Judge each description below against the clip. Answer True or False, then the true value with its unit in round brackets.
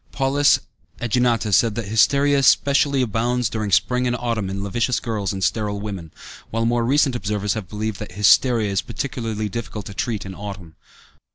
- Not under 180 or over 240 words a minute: False (170 wpm)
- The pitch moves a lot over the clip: False (3.3 semitones)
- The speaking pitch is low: True (110 Hz)